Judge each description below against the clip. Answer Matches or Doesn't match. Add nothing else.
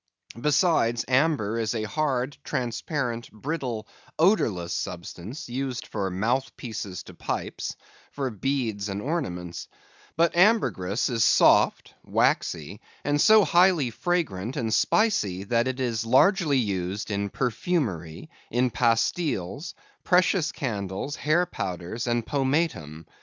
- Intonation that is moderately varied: Doesn't match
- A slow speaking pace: Matches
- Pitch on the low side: Matches